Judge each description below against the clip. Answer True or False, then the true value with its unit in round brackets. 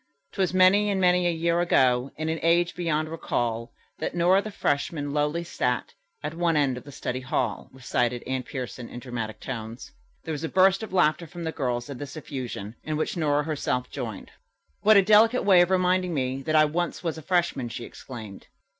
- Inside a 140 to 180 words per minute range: False (200 wpm)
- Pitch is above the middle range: False (155 Hz)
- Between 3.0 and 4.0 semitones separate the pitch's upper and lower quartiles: False (5.5 semitones)